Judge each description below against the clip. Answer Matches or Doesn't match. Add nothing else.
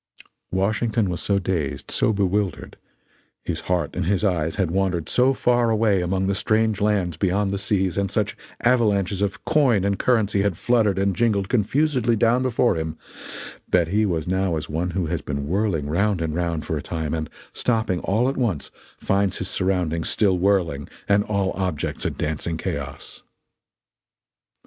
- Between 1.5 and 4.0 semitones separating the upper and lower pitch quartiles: Matches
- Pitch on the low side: Matches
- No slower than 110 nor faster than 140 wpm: Doesn't match